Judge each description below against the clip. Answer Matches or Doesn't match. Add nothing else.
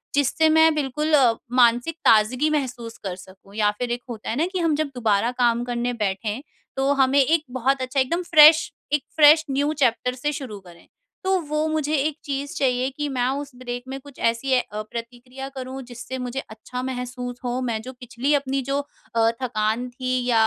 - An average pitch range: Matches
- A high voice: Matches